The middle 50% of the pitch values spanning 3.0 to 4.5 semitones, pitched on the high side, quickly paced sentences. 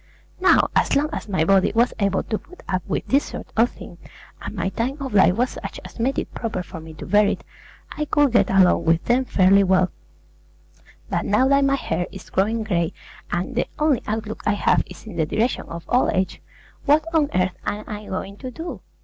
No: wide, 5.6 semitones; high, 210 Hz; fast, 215 wpm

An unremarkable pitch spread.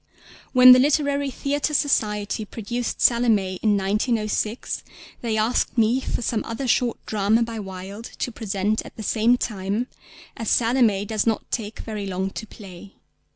Yes: average, 3.1 semitones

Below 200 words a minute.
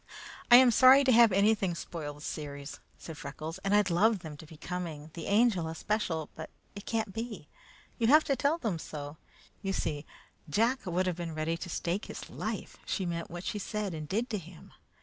No: fast, 205 wpm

